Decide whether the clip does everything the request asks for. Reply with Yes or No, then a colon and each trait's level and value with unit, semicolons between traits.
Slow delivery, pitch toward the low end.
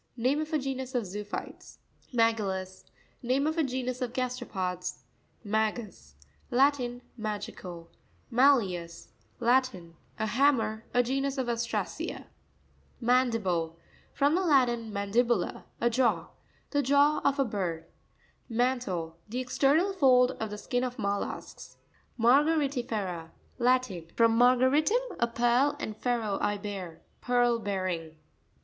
No: slow, 105 wpm; high, 240 Hz